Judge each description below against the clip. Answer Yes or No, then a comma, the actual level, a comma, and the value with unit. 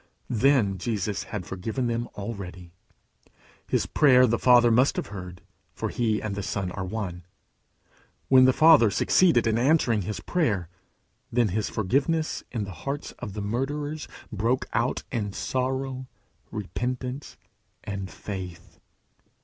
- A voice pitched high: No, low, 115 Hz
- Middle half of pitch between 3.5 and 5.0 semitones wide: Yes, average, 4.6 semitones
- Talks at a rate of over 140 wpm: No, slow, 135 wpm